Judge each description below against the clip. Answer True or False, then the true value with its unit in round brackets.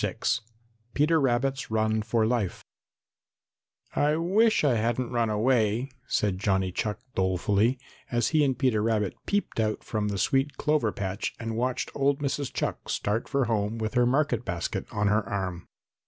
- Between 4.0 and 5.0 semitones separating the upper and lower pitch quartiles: True (4.4 semitones)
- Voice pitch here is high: False (115 Hz)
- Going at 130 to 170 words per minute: True (160 wpm)